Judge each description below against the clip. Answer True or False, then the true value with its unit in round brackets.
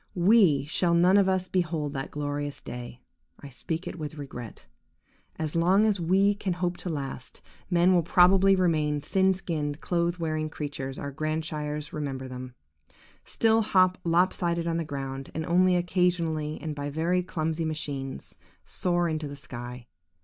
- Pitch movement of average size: True (3.7 semitones)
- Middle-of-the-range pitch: True (160 Hz)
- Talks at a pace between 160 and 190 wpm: True (165 wpm)